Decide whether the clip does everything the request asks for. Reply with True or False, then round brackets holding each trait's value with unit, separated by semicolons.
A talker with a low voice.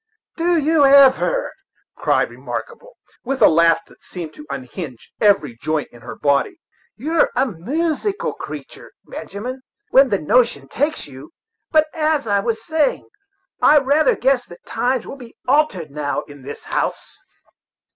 False (255 Hz)